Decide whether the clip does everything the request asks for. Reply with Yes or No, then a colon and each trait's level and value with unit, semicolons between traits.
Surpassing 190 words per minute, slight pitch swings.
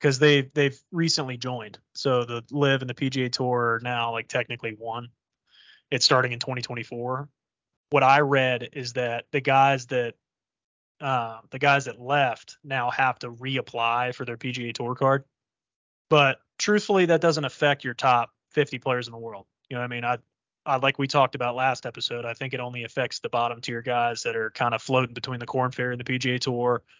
Yes: average, 200 wpm; narrow, 2.2 semitones